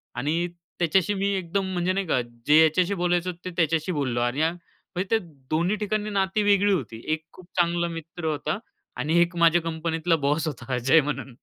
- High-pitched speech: No, medium, 170 Hz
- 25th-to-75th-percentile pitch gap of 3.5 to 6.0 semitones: No, average, 3.0 semitones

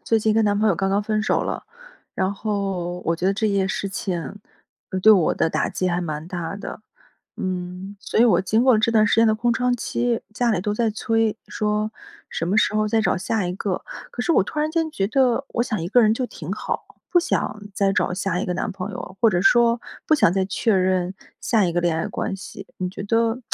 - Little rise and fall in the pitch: No, average, 3.4 semitones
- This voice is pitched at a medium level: No, high, 205 Hz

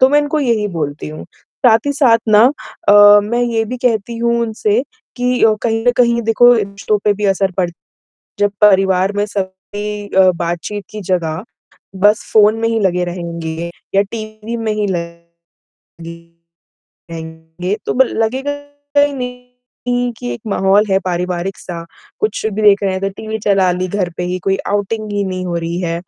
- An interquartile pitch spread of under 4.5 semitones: Yes, average, 3.7 semitones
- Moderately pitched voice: No, high, 205 Hz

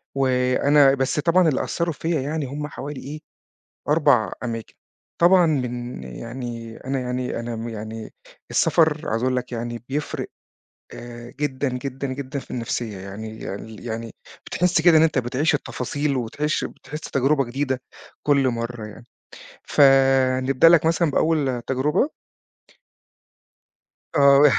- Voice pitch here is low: Yes, low, 130 Hz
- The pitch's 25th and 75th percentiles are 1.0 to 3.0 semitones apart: No, average, 3.6 semitones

